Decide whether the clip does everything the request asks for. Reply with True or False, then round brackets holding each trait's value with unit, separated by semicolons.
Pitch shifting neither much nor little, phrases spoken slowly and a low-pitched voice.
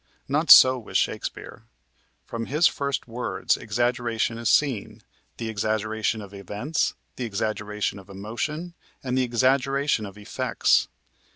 True (3.7 semitones; 125 wpm; 115 Hz)